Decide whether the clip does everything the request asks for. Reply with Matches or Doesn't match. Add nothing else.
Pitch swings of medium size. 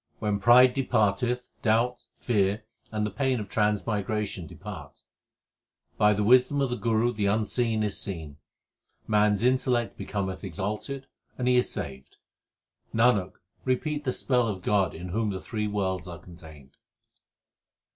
Matches